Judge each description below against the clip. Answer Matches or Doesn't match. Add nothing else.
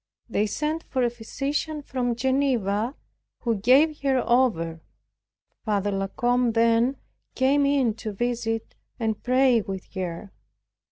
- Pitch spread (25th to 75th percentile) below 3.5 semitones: Doesn't match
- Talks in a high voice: Matches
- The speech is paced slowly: Matches